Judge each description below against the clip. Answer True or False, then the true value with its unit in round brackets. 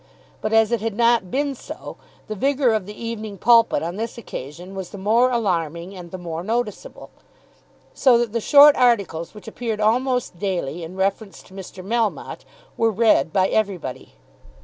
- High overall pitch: True (215 Hz)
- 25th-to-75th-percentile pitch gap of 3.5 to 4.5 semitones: True (4.0 semitones)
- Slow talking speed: False (170 wpm)